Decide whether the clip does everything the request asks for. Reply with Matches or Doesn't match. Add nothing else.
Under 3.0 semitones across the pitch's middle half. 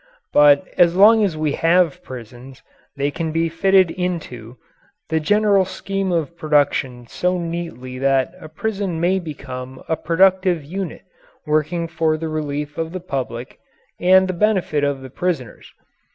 Doesn't match